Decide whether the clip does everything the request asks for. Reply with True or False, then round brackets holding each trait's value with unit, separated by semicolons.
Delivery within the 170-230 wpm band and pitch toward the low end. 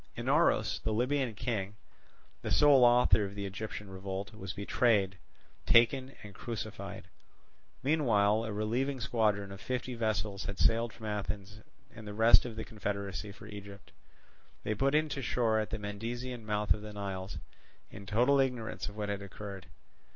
False (160 wpm; 105 Hz)